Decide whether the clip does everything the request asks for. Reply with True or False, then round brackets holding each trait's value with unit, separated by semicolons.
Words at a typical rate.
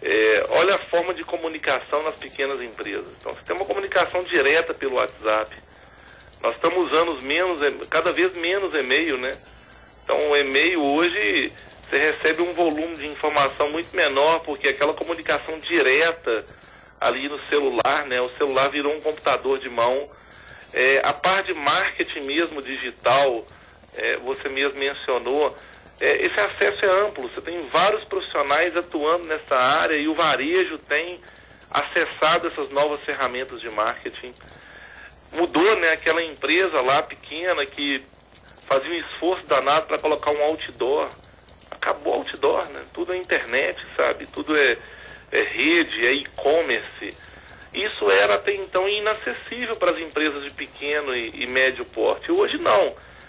True (145 wpm)